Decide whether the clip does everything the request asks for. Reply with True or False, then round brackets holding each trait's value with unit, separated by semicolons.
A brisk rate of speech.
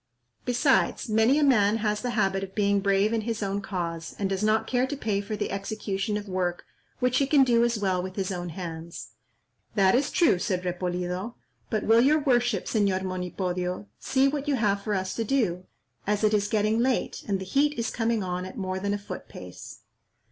True (210 wpm)